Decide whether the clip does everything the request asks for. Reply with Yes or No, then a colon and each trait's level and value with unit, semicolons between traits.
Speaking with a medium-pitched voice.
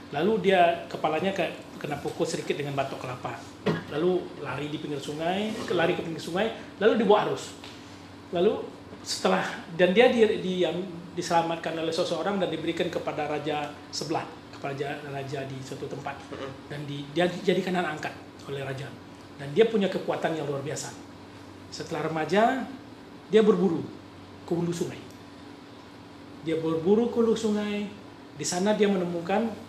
Yes: medium, 165 Hz